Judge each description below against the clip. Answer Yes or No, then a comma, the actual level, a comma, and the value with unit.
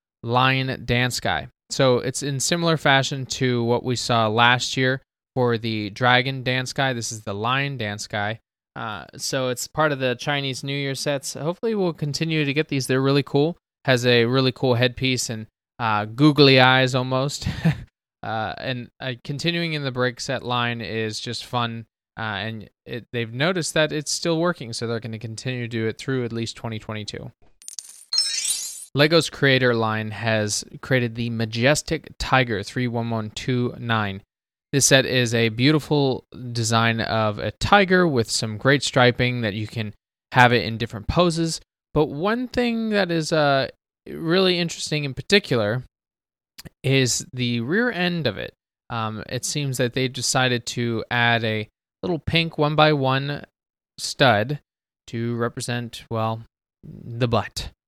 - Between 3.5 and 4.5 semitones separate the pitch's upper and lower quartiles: Yes, average, 3.8 semitones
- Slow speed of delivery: No, average, 160 wpm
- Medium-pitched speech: No, low, 125 Hz